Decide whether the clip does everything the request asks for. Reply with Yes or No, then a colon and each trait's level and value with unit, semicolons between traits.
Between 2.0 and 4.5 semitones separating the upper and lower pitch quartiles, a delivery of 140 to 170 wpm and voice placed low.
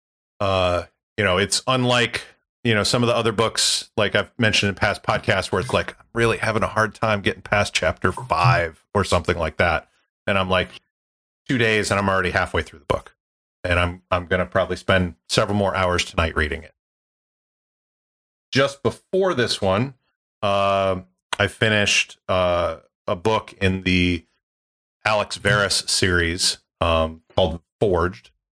Yes: average, 3.7 semitones; average, 160 wpm; very low, 95 Hz